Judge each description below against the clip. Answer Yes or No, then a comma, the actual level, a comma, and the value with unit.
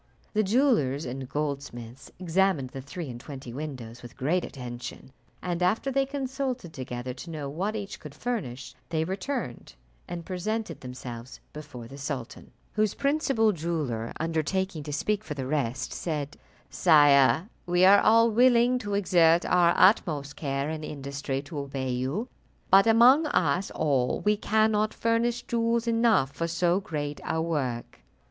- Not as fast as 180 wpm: Yes, average, 155 wpm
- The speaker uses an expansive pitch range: Yes, wide, 7.6 semitones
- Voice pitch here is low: No, medium, 160 Hz